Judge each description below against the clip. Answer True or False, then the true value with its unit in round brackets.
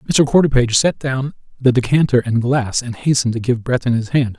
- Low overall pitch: True (125 Hz)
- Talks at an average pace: True (190 wpm)